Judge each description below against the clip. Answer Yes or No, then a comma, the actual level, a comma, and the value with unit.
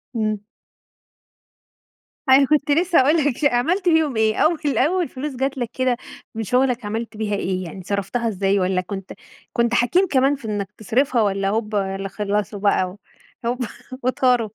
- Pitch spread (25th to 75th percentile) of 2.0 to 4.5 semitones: No, average, 5.0 semitones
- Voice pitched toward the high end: Yes, high, 235 Hz